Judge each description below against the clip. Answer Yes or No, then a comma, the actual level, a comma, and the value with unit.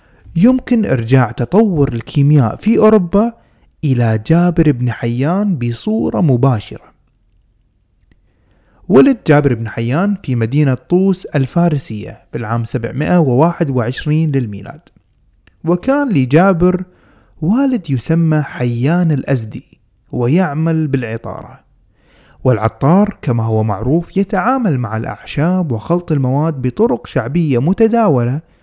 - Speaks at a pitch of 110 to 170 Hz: Yes, medium, 140 Hz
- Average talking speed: Yes, average, 90 wpm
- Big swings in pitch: Yes, wide, 6.7 semitones